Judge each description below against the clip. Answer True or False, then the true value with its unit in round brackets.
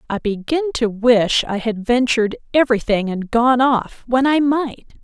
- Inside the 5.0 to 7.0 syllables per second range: False (4.6 syllables/s)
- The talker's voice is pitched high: True (240 Hz)